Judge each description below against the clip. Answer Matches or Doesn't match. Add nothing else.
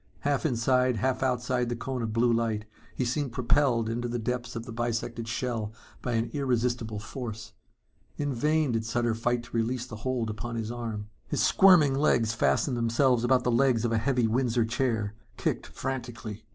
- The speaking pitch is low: Matches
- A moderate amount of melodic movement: Doesn't match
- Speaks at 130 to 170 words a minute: Doesn't match